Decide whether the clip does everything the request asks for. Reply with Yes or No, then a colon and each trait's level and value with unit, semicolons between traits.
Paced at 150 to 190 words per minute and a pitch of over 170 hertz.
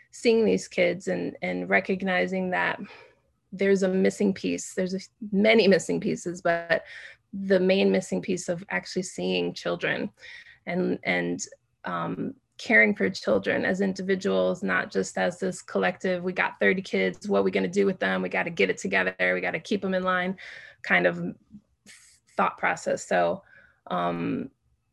Yes: average, 165 wpm; medium, 185 Hz